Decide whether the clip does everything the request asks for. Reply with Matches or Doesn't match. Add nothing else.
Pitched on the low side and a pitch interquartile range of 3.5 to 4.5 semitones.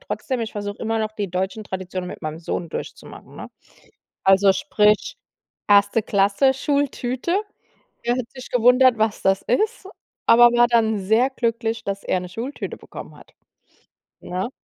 Doesn't match